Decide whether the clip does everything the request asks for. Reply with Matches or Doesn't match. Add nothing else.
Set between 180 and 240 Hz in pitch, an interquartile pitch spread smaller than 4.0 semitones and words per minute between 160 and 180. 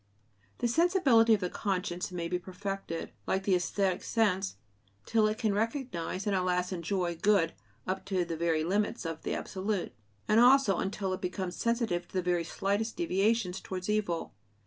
Matches